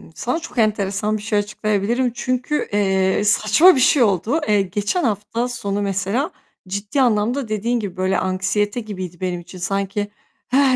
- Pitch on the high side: Yes, high, 210 Hz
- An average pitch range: Yes, average, 3.7 semitones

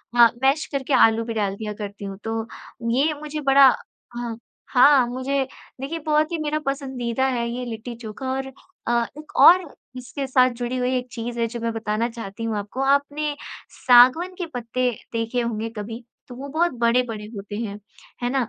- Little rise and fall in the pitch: No, average, 3.1 semitones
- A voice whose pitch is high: Yes, high, 245 Hz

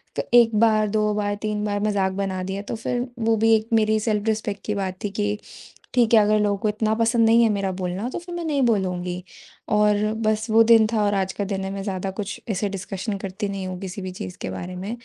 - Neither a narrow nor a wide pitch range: No, narrow, 2.3 semitones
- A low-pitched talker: No, high, 210 Hz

